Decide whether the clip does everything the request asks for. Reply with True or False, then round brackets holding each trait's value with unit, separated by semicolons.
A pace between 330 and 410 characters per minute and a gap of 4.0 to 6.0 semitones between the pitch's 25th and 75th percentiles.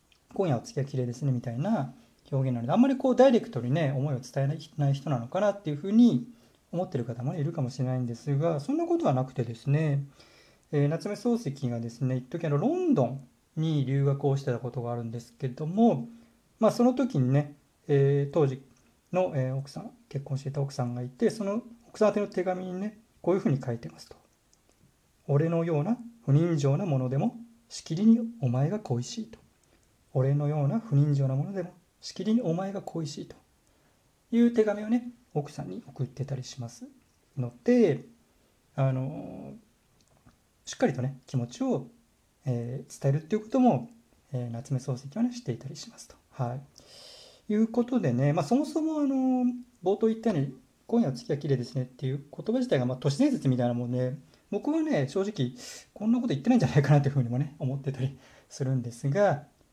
False (385 characters per minute; 8.4 semitones)